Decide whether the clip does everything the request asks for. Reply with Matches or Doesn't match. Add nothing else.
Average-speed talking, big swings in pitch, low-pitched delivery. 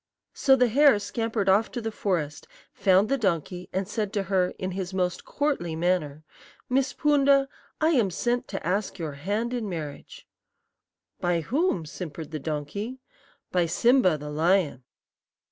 Doesn't match